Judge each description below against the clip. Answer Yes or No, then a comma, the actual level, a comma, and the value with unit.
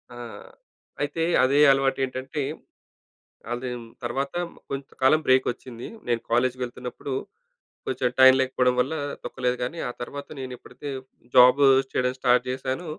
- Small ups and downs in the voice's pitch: Yes, narrow, 1.4 semitones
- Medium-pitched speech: No, low, 130 Hz